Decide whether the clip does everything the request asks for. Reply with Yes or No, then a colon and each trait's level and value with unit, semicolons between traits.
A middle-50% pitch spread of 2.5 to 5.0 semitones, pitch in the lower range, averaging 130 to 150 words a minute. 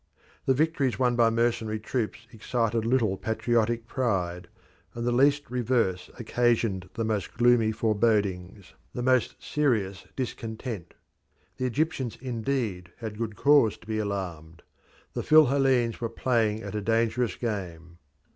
Yes: average, 2.9 semitones; low, 115 Hz; slow, 135 wpm